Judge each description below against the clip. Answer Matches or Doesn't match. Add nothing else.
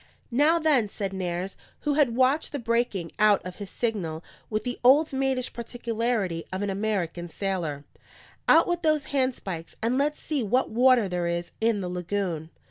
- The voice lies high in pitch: Matches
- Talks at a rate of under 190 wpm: Matches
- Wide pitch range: Matches